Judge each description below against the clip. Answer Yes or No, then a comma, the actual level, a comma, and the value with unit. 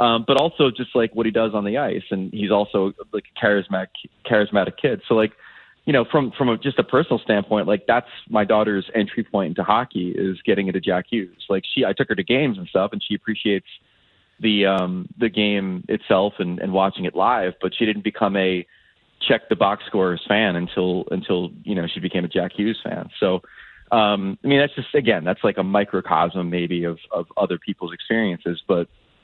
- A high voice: No, low, 105 Hz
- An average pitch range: Yes, average, 3.4 semitones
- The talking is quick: Yes, fast, 210 wpm